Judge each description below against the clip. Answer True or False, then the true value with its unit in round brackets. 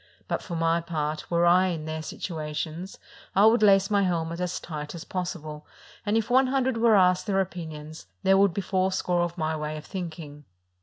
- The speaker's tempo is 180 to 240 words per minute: True (200 wpm)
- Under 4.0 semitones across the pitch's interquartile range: True (3.5 semitones)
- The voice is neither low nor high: True (175 Hz)